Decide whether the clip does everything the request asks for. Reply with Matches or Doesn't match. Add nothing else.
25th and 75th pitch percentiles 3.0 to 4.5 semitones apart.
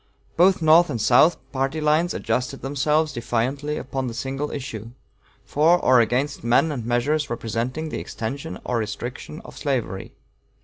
Matches